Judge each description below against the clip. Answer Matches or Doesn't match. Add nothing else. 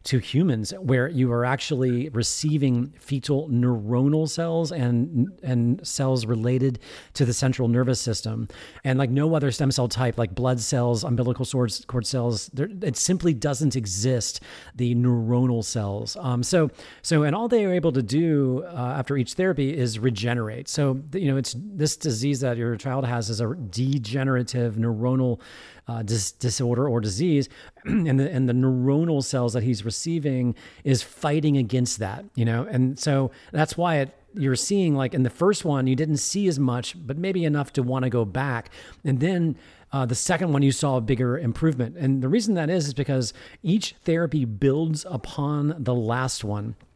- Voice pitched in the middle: Doesn't match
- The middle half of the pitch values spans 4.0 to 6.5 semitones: Doesn't match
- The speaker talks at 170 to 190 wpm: Matches